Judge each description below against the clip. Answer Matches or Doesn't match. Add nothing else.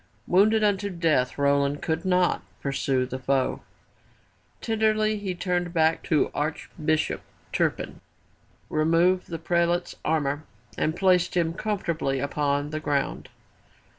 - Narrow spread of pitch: Doesn't match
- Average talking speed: Doesn't match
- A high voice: Doesn't match